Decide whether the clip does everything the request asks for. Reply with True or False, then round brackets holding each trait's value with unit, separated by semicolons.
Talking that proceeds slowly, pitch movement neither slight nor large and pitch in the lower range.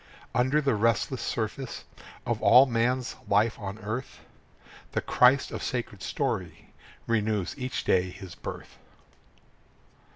True (120 wpm; 3.6 semitones; 115 Hz)